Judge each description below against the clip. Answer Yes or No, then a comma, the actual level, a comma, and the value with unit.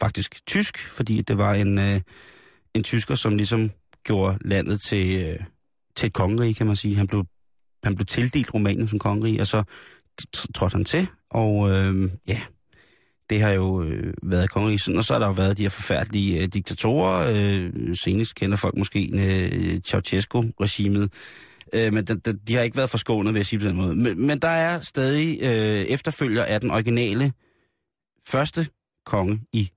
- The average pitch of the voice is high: No, low, 105 Hz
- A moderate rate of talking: Yes, average, 175 wpm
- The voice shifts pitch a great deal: No, average, 2.9 semitones